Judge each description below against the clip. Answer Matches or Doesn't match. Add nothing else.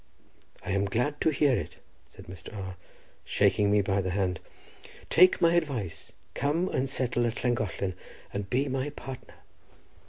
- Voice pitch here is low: Matches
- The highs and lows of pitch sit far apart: Matches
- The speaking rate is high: Doesn't match